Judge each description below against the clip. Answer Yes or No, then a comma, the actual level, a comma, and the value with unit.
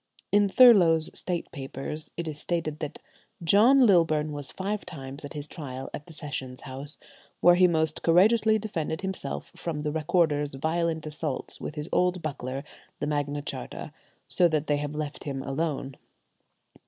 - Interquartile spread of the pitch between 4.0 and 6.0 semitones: No, average, 3.1 semitones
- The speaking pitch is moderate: Yes, medium, 155 Hz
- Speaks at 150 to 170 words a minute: Yes, average, 160 wpm